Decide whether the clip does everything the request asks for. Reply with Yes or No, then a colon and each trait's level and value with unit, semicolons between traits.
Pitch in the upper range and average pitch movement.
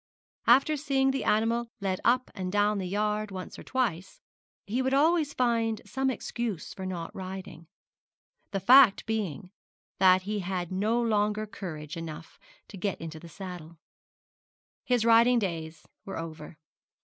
Yes: high, 205 Hz; average, 4.7 semitones